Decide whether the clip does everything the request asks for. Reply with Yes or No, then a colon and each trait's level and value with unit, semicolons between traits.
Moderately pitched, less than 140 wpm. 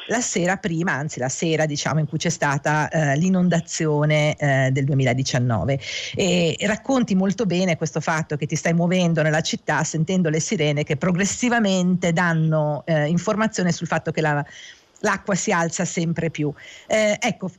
No: medium, 165 Hz; average, 165 wpm